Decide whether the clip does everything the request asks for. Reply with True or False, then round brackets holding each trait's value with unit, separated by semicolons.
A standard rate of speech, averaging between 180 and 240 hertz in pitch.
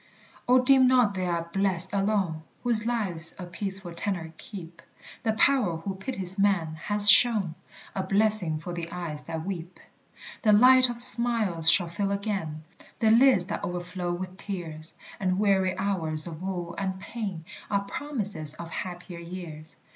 True (155 wpm; 190 Hz)